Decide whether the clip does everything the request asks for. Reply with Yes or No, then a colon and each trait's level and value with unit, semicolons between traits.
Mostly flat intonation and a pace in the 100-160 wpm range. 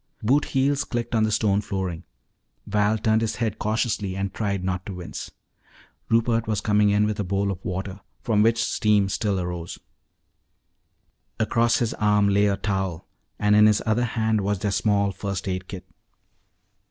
No: narrow, 2.1 semitones; average, 170 wpm